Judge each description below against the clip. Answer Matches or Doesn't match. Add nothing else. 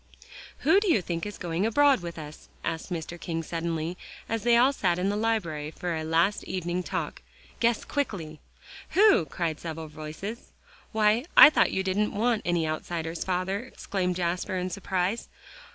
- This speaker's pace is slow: Doesn't match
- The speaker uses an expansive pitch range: Doesn't match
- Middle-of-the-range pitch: Matches